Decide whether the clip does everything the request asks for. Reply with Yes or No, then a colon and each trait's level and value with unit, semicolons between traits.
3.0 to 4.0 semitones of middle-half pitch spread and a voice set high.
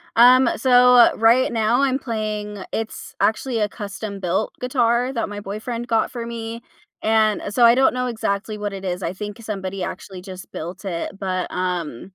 Yes: average, 3.4 semitones; high, 215 Hz